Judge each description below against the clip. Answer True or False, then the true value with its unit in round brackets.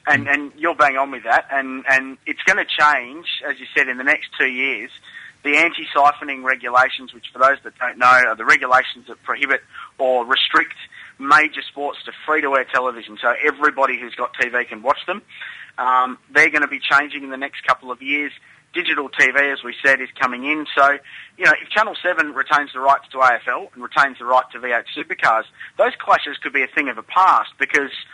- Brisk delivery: True (210 wpm)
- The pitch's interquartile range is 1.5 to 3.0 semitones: True (2.4 semitones)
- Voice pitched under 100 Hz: False (135 Hz)